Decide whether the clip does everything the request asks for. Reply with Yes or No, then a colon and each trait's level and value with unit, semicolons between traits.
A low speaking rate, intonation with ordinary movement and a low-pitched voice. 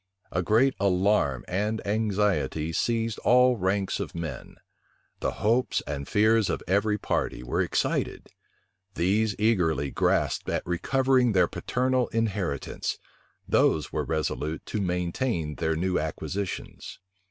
Yes: slow, 120 wpm; average, 5.0 semitones; low, 100 Hz